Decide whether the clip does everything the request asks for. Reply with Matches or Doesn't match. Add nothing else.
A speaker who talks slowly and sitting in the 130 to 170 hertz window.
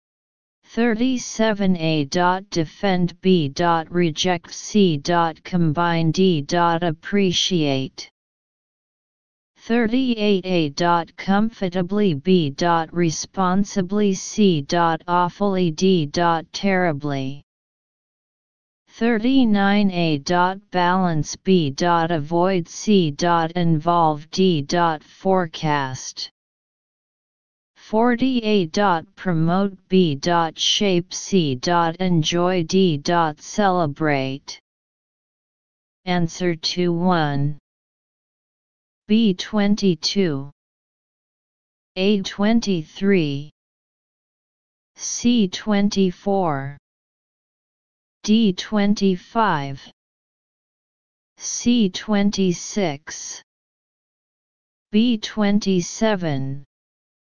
Doesn't match